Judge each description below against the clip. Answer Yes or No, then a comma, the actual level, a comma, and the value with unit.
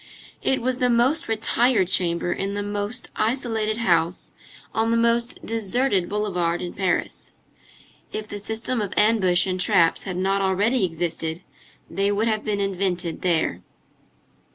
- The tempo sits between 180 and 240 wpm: No, average, 145 wpm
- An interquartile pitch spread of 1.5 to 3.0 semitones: No, average, 3.8 semitones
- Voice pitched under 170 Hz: No, high, 205 Hz